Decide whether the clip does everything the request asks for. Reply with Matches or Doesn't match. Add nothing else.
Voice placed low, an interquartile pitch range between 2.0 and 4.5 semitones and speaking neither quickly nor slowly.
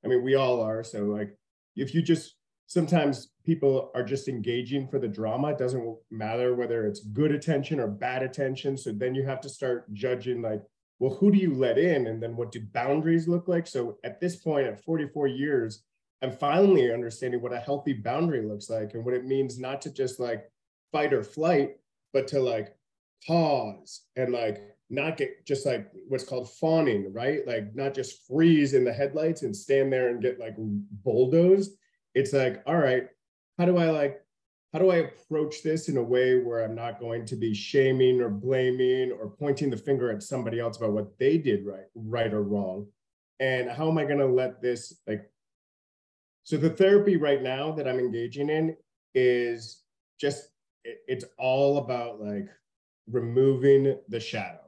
Matches